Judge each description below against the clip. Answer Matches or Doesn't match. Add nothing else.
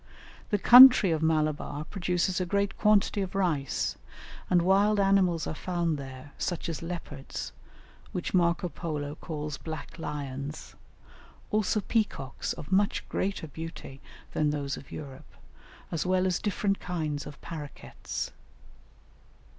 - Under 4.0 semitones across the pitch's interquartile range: Doesn't match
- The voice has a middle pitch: Matches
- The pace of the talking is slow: Matches